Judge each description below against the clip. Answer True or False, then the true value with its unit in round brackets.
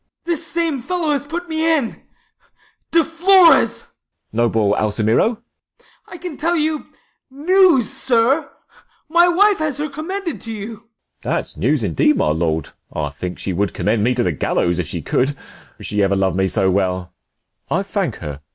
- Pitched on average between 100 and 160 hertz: False (245 Hz)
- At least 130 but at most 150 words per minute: False (180 wpm)